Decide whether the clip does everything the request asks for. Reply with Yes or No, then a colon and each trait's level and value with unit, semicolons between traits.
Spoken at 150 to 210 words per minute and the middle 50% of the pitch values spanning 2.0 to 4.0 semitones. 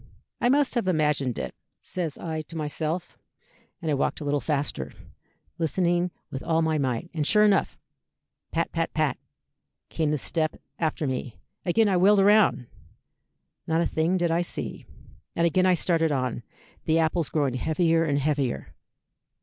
Yes: average, 160 wpm; average, 3.1 semitones